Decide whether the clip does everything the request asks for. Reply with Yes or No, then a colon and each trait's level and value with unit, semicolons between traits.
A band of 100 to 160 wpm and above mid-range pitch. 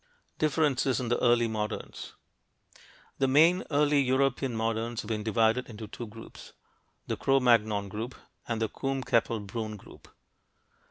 No: average, 145 wpm; low, 120 Hz